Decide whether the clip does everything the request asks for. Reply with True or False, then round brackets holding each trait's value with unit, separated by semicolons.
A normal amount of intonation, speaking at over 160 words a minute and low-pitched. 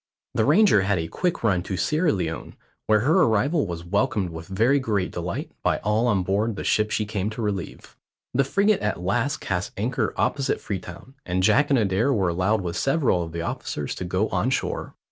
False (5.9 semitones; 200 wpm; 105 Hz)